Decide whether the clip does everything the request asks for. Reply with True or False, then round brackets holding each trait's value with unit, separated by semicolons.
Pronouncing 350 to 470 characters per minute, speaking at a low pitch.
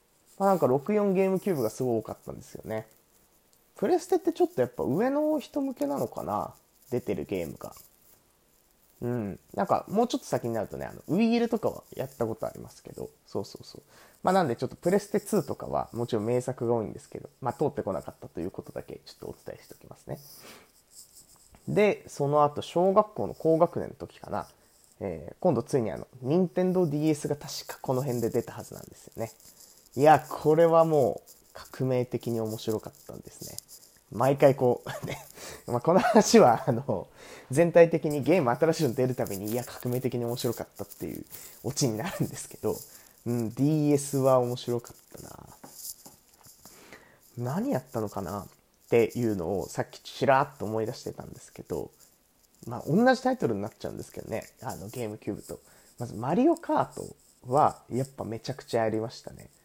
True (380 characters per minute; 130 Hz)